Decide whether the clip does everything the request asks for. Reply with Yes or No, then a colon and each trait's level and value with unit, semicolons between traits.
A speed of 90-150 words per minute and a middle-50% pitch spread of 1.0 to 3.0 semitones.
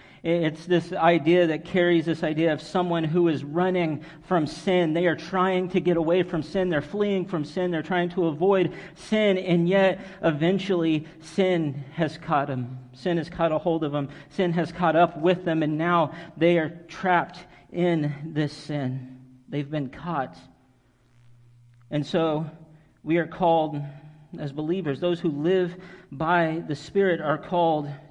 No: average, 165 wpm; average, 2.7 semitones